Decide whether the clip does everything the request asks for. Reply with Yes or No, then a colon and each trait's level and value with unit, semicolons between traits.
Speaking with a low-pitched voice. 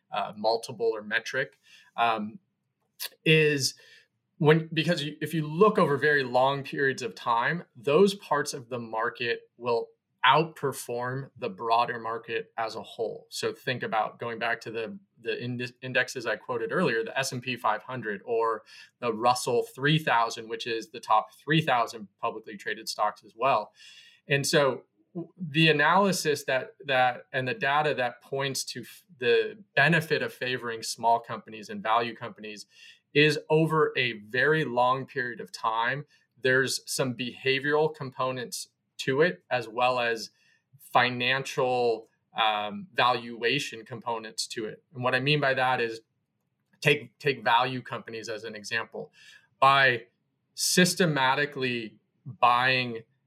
Yes: low, 130 Hz